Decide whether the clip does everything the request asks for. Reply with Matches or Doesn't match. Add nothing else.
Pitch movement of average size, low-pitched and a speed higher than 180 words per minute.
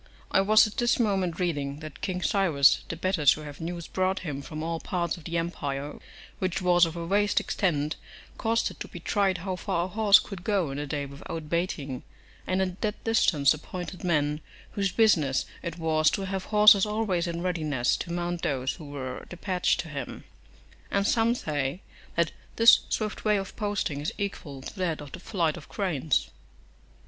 Doesn't match